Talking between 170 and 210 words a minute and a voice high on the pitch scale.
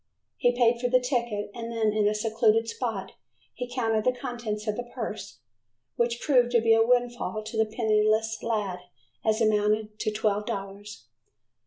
Yes: average, 175 wpm; high, 225 Hz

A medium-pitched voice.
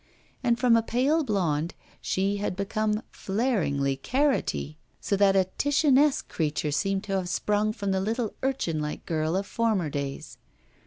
No: high, 200 Hz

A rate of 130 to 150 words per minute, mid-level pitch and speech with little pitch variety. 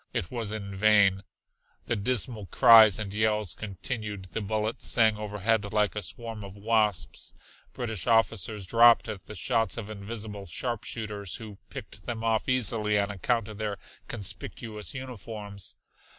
No: average, 145 wpm; low, 105 Hz; narrow, 1.9 semitones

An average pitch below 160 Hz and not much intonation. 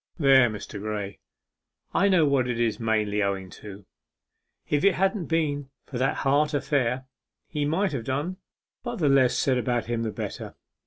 No: low, 135 Hz; average, 4.9 semitones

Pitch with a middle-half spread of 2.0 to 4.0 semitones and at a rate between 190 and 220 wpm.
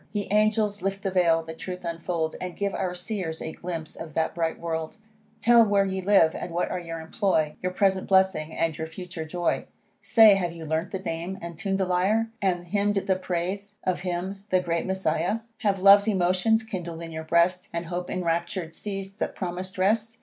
Yes: average, 2.8 semitones; average, 200 wpm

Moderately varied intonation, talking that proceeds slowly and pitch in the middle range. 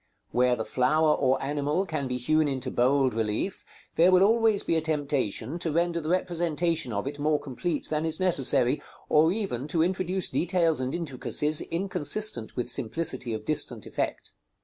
No: average, 4.7 semitones; average, 170 wpm; medium, 155 Hz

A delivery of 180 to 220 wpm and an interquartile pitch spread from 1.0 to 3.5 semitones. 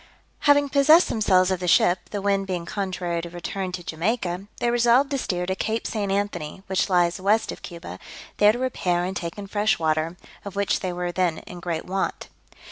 Yes: fast, 205 wpm; average, 2.9 semitones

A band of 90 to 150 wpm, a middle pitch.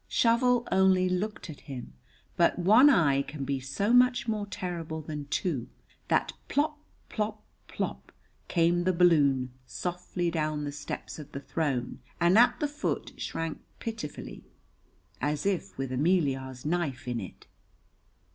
Yes: average, 140 wpm; medium, 170 Hz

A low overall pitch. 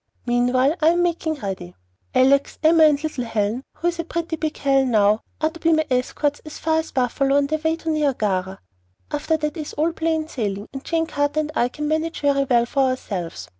No: very high, 290 Hz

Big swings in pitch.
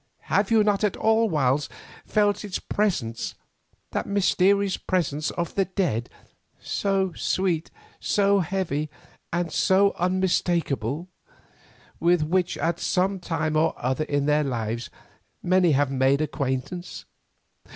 No: average, 4.8 semitones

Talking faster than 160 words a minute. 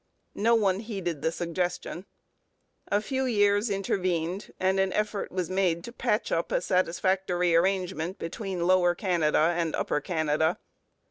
No: average, 140 wpm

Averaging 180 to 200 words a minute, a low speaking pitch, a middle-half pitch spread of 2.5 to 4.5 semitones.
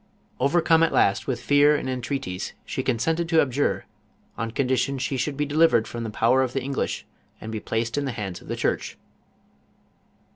Yes: average, 190 wpm; low, 130 Hz; average, 3.9 semitones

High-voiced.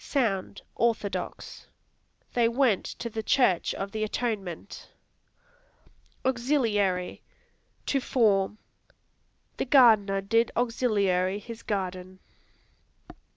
Yes: high, 215 Hz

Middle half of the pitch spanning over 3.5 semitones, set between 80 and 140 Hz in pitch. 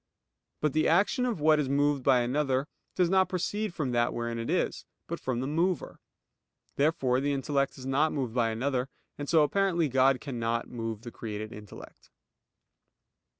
Yes: average, 4.3 semitones; low, 135 Hz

